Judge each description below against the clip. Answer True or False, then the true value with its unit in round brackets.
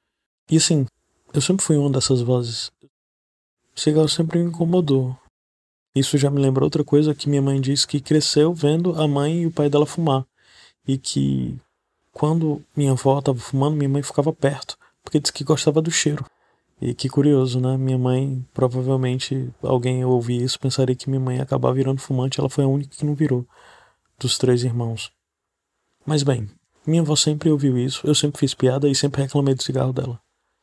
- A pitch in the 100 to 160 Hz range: True (135 Hz)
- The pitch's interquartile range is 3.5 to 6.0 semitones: False (2.6 semitones)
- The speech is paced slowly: False (185 wpm)